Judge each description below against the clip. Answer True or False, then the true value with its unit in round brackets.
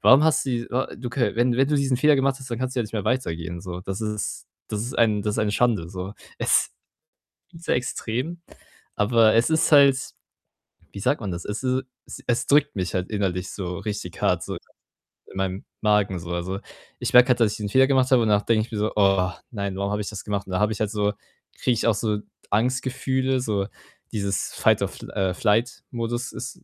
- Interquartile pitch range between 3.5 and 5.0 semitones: True (4.2 semitones)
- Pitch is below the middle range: True (110 Hz)